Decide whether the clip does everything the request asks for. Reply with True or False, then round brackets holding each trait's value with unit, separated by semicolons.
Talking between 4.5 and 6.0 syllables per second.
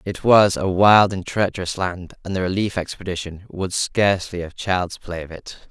True (4.8 syllables/s)